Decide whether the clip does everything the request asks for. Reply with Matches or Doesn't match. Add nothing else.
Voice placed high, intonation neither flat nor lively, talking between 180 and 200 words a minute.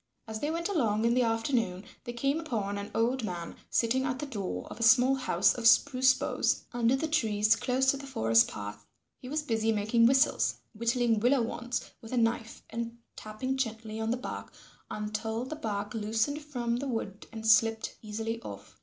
Matches